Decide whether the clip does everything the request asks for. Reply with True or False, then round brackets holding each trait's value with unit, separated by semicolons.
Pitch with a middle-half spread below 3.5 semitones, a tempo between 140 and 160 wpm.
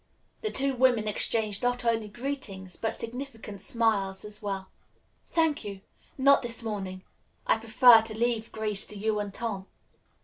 True (3.0 semitones; 150 wpm)